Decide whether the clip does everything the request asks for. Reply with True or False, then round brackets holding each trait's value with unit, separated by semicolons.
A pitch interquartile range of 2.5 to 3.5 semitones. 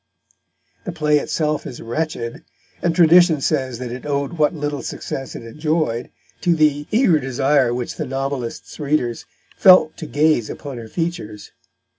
False (4.0 semitones)